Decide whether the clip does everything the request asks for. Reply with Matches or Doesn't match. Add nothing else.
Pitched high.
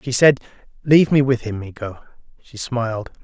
Doesn't match